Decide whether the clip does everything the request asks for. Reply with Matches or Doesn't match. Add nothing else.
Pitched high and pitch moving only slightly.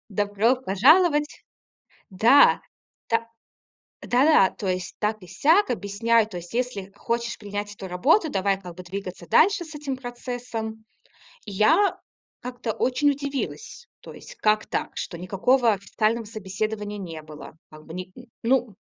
Doesn't match